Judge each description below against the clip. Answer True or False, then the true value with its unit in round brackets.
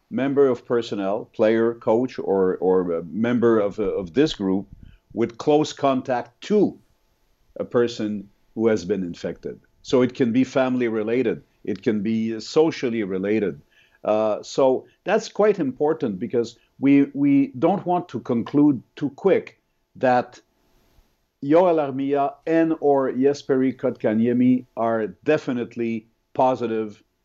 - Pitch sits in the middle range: False (125 Hz)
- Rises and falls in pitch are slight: False (4.2 semitones)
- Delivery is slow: True (125 wpm)